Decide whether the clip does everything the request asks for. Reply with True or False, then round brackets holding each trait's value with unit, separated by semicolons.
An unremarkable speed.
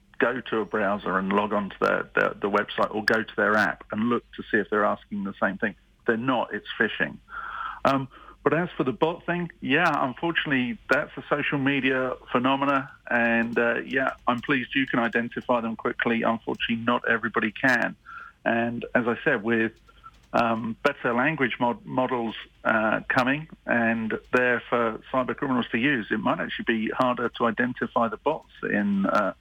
True (180 wpm)